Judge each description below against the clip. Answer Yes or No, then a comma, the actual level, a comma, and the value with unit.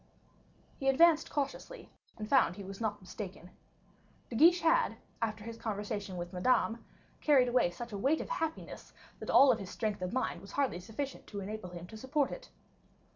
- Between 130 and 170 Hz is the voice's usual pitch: No, high, 225 Hz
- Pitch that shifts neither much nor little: No, wide, 5.8 semitones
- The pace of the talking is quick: No, average, 180 wpm